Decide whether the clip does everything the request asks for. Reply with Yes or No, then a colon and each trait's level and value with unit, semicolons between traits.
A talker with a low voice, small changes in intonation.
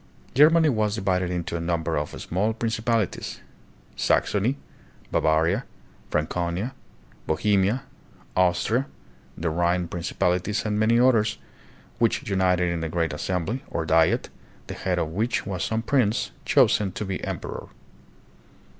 No: very low, 95 Hz; average, 4.5 semitones